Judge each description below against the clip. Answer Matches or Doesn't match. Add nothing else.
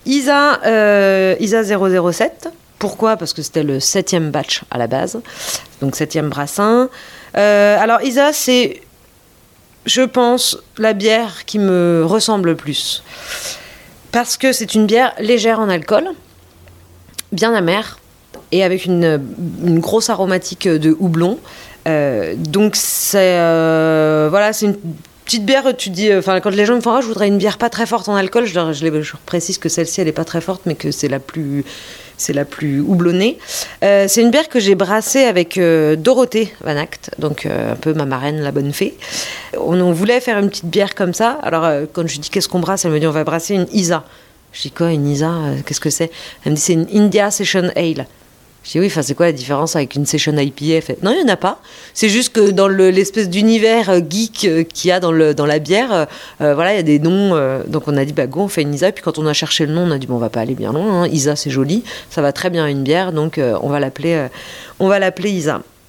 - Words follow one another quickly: Matches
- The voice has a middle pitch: Matches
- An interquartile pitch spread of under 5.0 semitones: Doesn't match